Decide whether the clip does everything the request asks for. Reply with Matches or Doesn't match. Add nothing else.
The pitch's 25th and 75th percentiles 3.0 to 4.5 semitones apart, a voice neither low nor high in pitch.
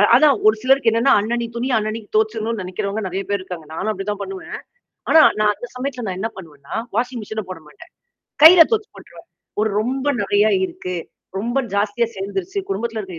Doesn't match